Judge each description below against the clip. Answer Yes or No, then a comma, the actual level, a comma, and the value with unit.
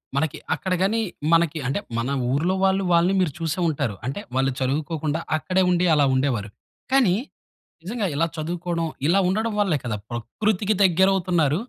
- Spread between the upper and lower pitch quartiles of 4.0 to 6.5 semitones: Yes, average, 4.9 semitones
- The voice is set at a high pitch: No, medium, 170 Hz